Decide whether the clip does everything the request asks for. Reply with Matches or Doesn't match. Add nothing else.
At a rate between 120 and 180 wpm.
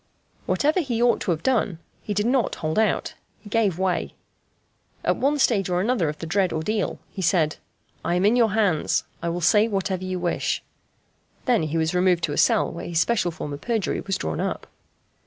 Doesn't match